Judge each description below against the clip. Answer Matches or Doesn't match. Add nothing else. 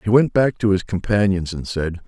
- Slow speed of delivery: Doesn't match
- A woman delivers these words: Doesn't match